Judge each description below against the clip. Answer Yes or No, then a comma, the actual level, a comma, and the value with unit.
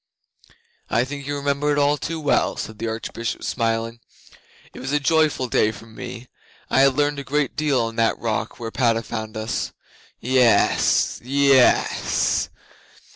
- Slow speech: No, average, 155 wpm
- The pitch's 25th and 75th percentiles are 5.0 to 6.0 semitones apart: No, average, 3.8 semitones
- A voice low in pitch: Yes, low, 130 Hz